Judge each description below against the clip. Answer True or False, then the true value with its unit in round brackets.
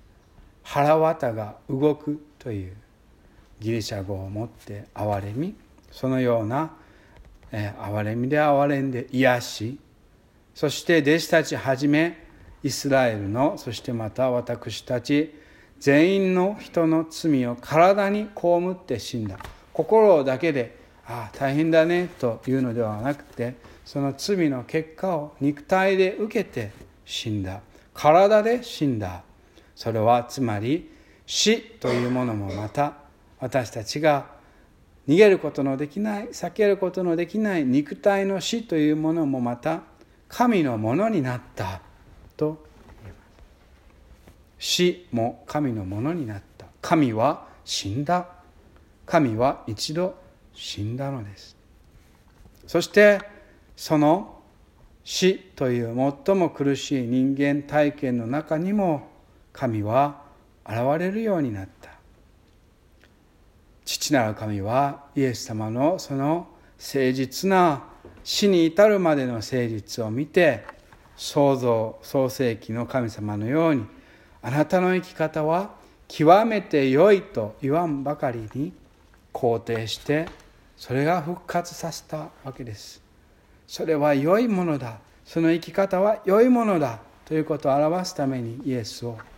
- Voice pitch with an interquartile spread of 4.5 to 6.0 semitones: False (6.6 semitones)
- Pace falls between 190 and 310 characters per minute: True (235 characters per minute)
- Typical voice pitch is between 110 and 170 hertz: True (140 Hz)